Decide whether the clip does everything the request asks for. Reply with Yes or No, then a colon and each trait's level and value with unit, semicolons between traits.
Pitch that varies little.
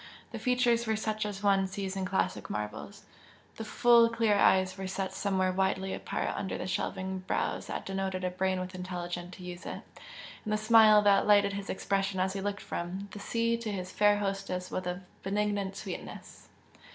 Yes: narrow, 1.9 semitones